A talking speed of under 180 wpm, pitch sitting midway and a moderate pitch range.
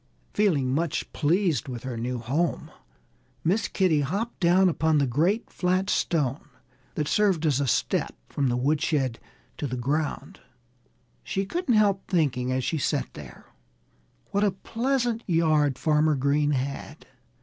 No: average, 145 wpm; medium, 155 Hz; wide, 5.7 semitones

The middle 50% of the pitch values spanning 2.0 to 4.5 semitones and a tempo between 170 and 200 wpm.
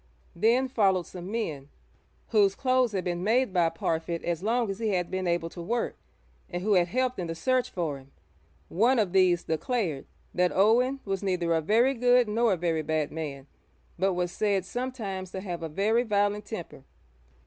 No: average, 4.9 semitones; average, 190 wpm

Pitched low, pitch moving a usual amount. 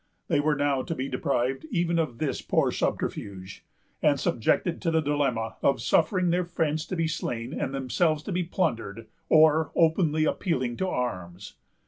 No: medium, 150 Hz; average, 4.8 semitones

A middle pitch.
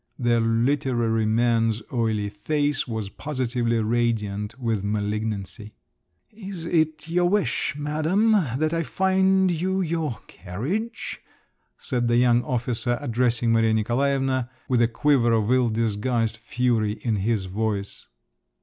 No: low, 120 Hz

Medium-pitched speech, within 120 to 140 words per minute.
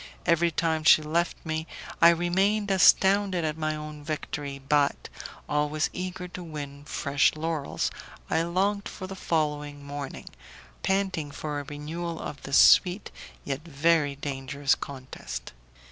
Yes: medium, 155 Hz; slow, 135 wpm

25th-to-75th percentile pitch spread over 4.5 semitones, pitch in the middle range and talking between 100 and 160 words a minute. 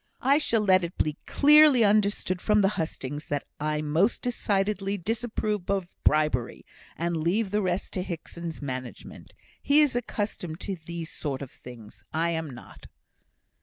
Yes: average, 5.3 semitones; medium, 180 Hz; average, 155 wpm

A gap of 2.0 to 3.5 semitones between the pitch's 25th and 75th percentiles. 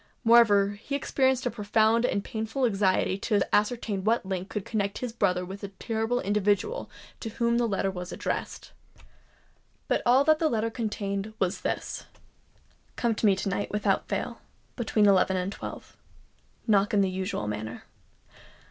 Yes: average, 3.0 semitones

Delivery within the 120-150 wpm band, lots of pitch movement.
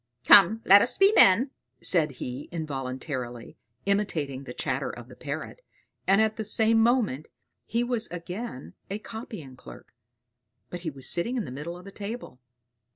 No: average, 160 wpm; wide, 8.0 semitones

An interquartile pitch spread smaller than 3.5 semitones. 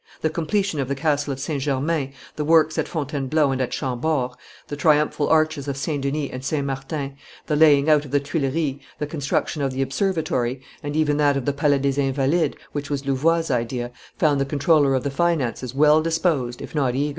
Yes: narrow, 2.4 semitones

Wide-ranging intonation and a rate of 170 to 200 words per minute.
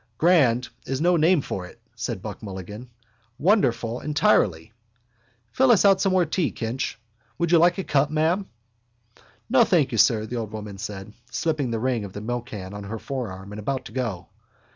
Yes: wide, 7.7 semitones; average, 185 wpm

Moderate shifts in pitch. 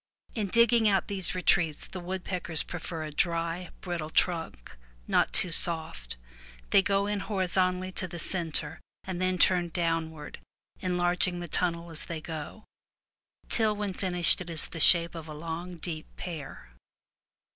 No: narrow, 2.2 semitones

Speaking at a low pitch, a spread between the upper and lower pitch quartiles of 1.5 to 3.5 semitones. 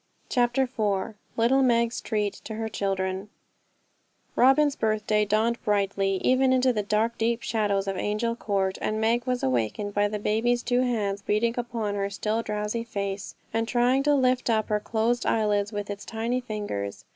No: high, 220 Hz; average, 2.8 semitones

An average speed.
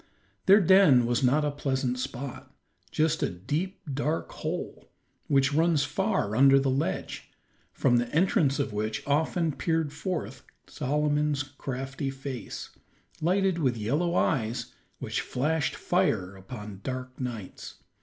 No: slow, 130 wpm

